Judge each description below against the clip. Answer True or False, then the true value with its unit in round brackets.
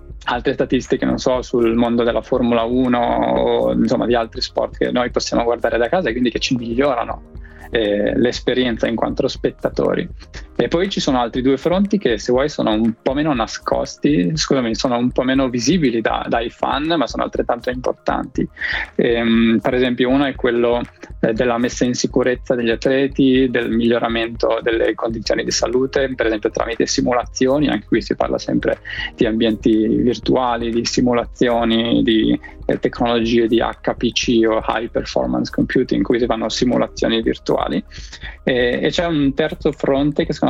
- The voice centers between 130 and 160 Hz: False (120 Hz)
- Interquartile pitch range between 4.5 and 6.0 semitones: False (2.4 semitones)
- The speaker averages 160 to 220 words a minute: True (165 wpm)